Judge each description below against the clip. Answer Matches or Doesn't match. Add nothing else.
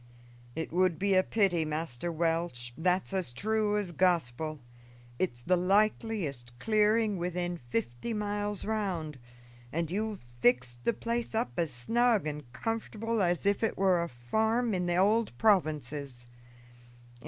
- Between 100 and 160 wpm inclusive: Matches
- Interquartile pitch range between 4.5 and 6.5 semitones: Matches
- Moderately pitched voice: Matches